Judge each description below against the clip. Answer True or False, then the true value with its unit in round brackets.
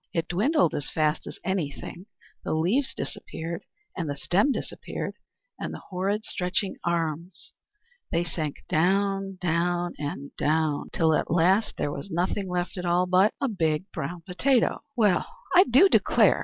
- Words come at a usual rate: True (155 wpm)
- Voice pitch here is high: False (175 Hz)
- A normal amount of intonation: True (3.4 semitones)